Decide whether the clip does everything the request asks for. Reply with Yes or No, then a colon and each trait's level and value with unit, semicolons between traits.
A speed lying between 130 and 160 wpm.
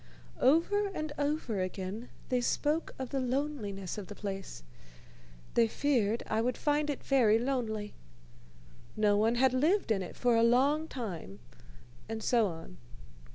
Yes: average, 150 wpm